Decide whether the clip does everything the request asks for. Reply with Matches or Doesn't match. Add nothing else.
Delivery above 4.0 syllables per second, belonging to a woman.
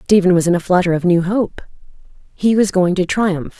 Matches